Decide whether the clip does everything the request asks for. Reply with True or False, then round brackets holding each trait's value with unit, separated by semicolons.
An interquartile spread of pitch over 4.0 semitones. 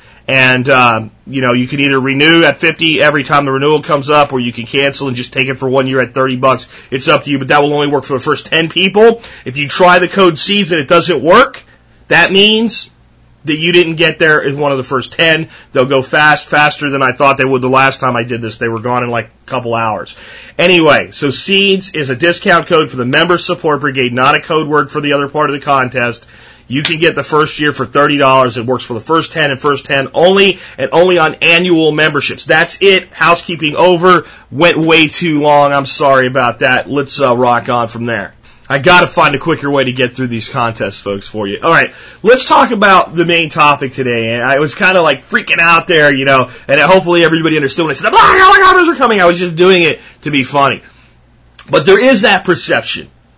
True (4.5 semitones)